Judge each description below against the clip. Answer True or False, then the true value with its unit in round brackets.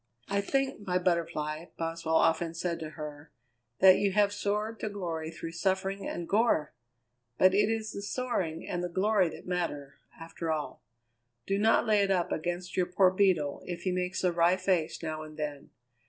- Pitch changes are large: False (3.4 semitones)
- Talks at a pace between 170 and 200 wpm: True (185 wpm)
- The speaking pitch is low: False (180 Hz)